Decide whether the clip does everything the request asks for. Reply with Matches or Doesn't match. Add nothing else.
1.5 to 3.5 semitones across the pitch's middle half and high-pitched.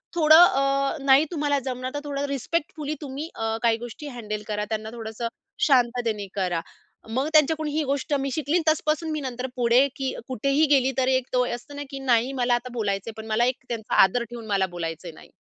Doesn't match